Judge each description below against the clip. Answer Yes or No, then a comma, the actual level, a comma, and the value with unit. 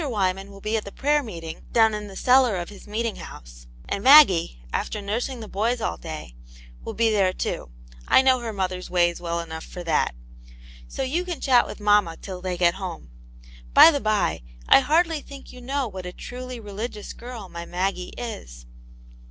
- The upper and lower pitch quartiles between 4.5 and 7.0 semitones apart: Yes, wide, 5.5 semitones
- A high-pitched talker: Yes, high, 205 Hz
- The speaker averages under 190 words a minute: No, average, 195 wpm